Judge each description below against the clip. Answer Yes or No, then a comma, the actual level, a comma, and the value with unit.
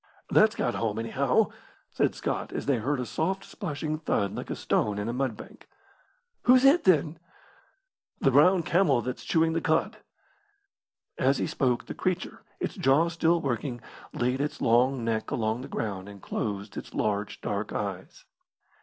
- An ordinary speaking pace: Yes, average, 165 wpm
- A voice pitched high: No, low, 130 Hz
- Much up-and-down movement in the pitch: Yes, wide, 6.5 semitones